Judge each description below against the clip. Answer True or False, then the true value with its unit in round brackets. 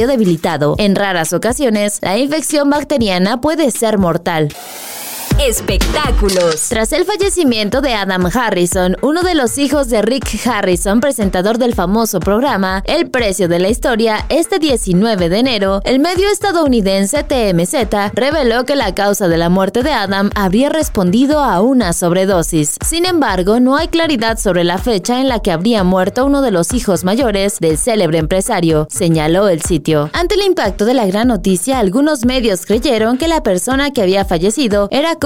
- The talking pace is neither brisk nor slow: True (165 wpm)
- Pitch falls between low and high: False (215 Hz)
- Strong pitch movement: True (6.5 semitones)